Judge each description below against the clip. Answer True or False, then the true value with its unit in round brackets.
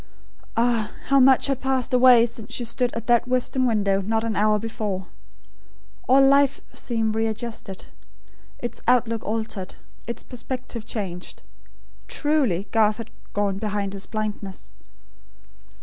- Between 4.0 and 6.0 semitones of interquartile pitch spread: False (3.1 semitones)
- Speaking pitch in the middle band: False (225 Hz)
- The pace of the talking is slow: True (130 wpm)